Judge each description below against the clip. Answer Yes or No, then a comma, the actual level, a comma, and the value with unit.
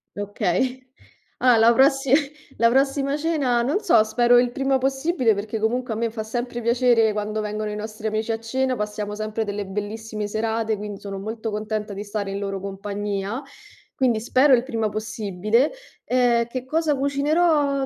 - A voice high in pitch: Yes, high, 225 Hz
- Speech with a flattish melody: No, average, 3.5 semitones